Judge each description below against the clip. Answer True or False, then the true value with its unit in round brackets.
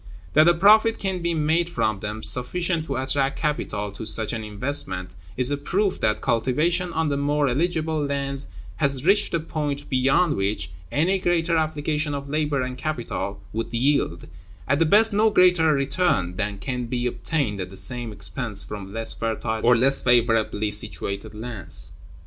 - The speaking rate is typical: True (170 wpm)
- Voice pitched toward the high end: False (140 Hz)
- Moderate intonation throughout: False (6.1 semitones)